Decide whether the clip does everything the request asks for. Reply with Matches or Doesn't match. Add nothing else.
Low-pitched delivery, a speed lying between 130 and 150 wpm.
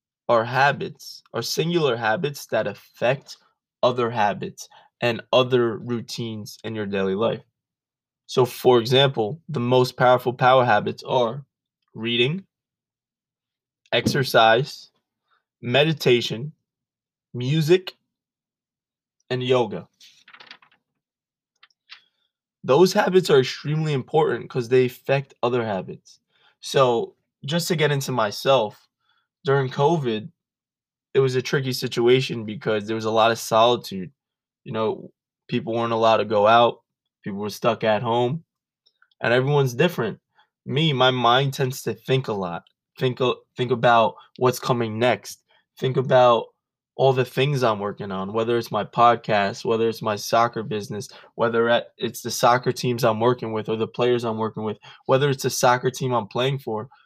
Matches